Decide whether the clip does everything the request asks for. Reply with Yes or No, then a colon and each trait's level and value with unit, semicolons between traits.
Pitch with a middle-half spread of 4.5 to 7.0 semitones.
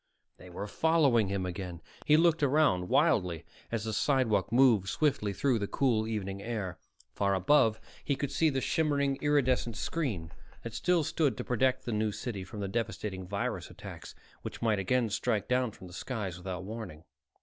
Yes: wide, 5.5 semitones